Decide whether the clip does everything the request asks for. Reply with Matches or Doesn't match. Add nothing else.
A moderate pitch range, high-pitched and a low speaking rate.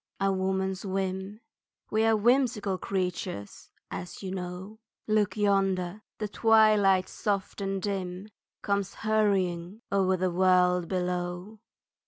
Doesn't match